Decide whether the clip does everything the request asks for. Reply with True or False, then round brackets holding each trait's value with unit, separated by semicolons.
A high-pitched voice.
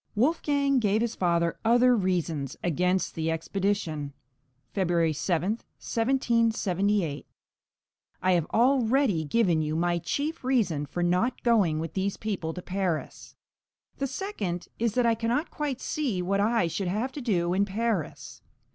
True (200 Hz)